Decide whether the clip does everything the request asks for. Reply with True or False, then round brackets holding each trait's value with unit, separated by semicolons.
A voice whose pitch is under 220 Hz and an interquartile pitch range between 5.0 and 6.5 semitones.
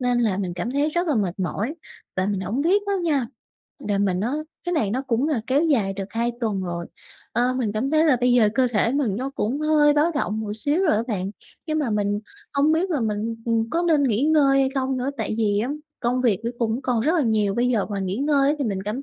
False (245 Hz; 5.5 semitones)